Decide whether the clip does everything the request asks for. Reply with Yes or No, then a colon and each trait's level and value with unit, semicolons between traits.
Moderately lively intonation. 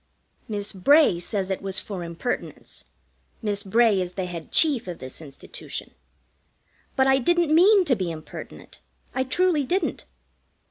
No: wide, 8.1 semitones